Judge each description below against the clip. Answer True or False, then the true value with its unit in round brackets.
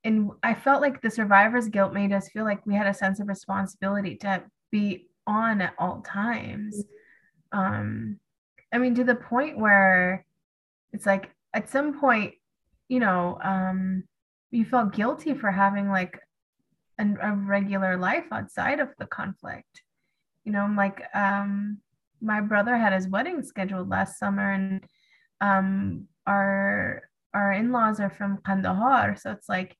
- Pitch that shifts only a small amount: True (2.3 semitones)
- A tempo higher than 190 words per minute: False (155 wpm)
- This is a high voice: True (200 Hz)